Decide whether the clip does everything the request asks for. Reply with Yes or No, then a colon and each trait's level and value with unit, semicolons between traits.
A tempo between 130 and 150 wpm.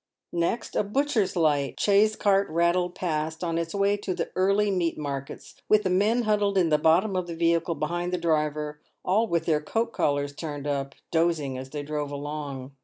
No: average, 190 wpm